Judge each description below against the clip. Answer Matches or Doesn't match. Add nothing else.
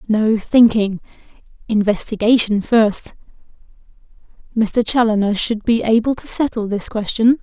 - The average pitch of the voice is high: Matches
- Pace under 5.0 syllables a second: Matches